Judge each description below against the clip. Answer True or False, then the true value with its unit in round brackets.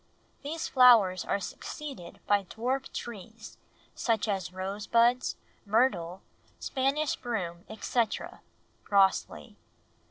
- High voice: True (220 Hz)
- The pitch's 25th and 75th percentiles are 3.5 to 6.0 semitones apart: True (4.7 semitones)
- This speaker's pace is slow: True (95 wpm)